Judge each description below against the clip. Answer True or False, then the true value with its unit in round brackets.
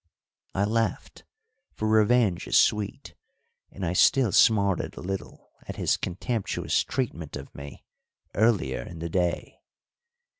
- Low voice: True (95 Hz)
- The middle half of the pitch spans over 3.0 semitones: True (4.1 semitones)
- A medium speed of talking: False (125 wpm)